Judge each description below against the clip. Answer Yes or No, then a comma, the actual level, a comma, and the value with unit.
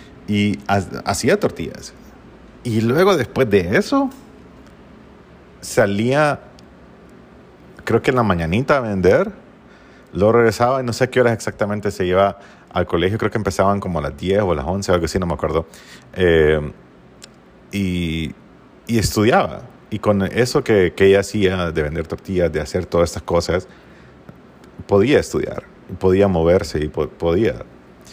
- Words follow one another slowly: No, average, 150 wpm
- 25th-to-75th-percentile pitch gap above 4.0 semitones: Yes, average, 4.4 semitones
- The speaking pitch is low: Yes, low, 100 Hz